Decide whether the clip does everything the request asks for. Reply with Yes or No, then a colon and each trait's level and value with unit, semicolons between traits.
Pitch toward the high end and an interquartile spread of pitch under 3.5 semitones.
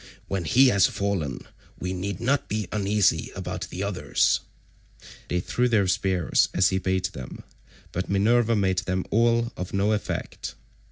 No: low, 100 Hz; average, 2.8 semitones